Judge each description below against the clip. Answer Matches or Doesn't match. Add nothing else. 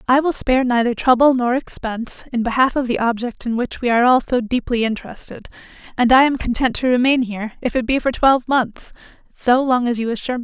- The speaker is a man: Doesn't match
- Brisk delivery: Matches